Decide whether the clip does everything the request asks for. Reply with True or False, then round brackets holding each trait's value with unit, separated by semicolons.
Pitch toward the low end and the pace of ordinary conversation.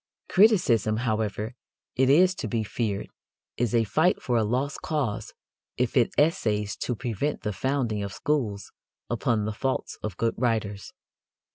True (115 Hz; 150 wpm)